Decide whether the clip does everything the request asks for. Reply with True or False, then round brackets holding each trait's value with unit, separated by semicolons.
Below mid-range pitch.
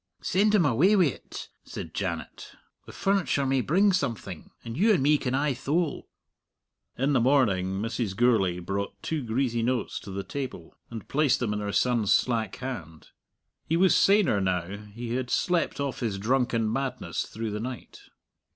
True (125 Hz)